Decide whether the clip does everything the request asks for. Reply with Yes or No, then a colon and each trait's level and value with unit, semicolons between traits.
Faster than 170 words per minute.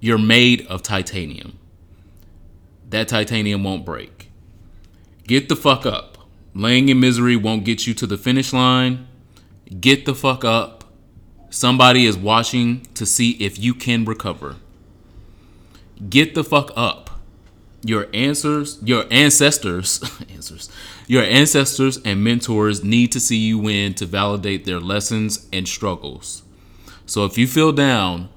No: slow, 135 wpm